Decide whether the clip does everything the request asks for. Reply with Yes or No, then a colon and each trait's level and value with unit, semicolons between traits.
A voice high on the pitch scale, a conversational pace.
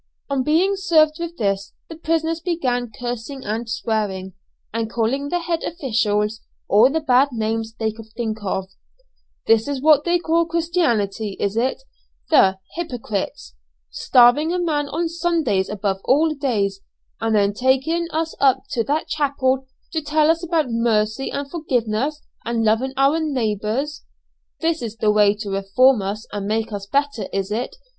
Yes: very high, 250 Hz; average, 160 wpm